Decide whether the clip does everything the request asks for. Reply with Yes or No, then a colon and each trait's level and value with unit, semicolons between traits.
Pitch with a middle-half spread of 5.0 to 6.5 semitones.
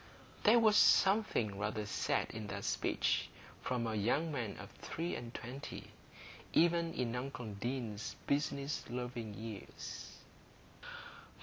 Yes: average, 5.3 semitones